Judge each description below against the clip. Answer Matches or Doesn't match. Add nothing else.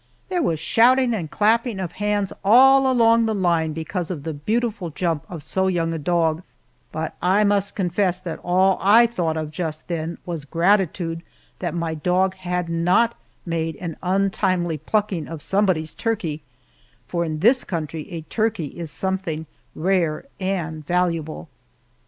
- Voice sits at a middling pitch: Matches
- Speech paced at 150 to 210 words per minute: Matches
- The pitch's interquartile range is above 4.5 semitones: Doesn't match